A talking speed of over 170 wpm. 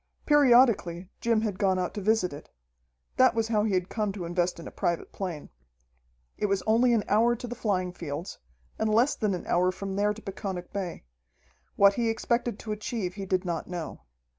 Yes: average, 200 wpm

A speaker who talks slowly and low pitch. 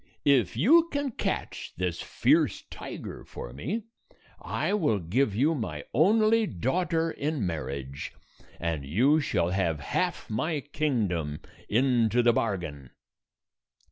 Yes: slow, 120 wpm; low, 120 Hz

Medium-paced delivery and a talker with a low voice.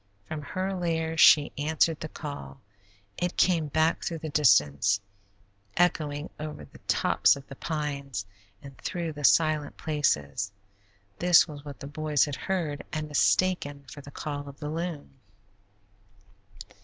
No: average, 145 wpm; medium, 150 Hz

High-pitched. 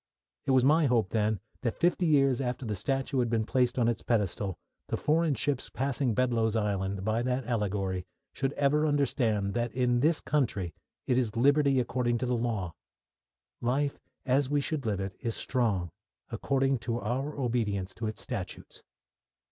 No: low, 120 Hz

